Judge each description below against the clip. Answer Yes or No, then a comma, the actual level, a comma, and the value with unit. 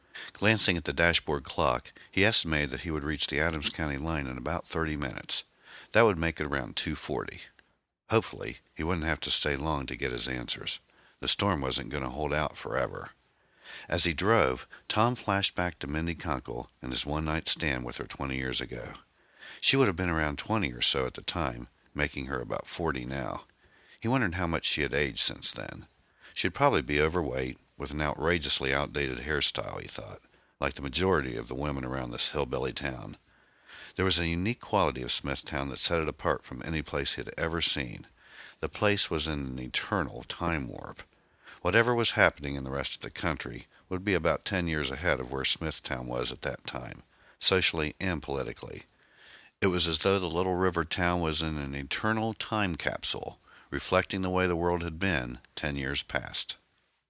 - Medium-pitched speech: No, very low, 75 Hz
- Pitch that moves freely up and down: No, average, 4.6 semitones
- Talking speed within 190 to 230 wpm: Yes, average, 195 wpm